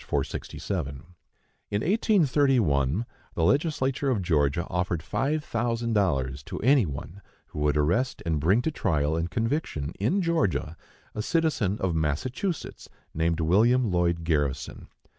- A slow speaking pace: Yes, slow, 130 wpm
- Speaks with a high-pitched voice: No, very low, 95 Hz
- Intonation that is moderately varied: No, wide, 8.6 semitones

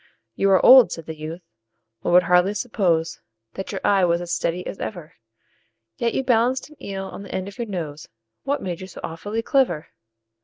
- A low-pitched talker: No, high, 190 Hz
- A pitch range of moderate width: Yes, average, 4.7 semitones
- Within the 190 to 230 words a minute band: Yes, average, 200 wpm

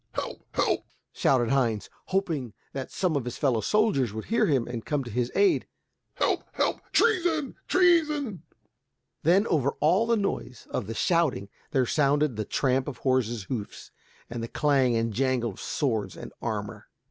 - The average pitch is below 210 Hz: Yes, low, 135 Hz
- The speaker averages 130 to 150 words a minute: No, average, 165 wpm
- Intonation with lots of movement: Yes, wide, 7.7 semitones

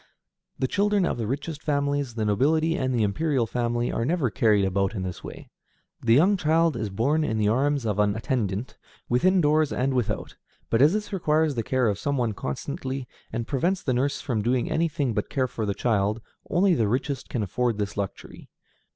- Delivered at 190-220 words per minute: Yes, average, 200 wpm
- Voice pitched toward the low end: Yes, low, 130 Hz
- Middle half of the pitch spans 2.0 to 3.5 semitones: No, wide, 5.4 semitones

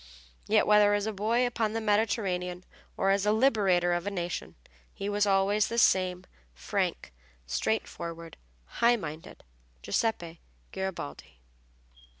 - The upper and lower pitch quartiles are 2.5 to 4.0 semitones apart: Yes, average, 3.5 semitones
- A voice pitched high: Yes, high, 200 Hz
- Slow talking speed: Yes, slow, 130 wpm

